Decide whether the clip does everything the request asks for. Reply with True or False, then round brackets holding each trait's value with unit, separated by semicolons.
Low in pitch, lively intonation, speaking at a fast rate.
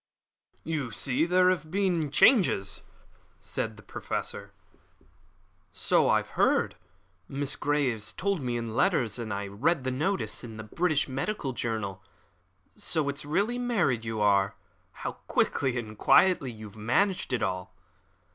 False (130 Hz; 7.6 semitones; 145 wpm)